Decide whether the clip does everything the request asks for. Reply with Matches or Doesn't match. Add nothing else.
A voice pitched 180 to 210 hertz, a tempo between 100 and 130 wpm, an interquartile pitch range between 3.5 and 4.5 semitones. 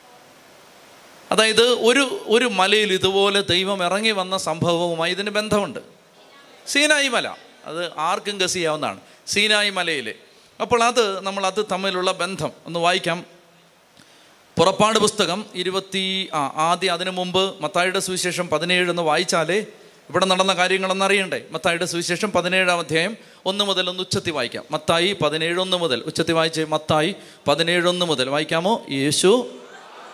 Doesn't match